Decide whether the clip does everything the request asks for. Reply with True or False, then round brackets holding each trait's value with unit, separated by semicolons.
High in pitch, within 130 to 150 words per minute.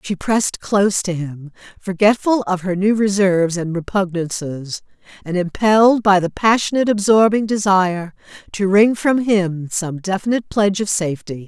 True (195 Hz; 145 wpm)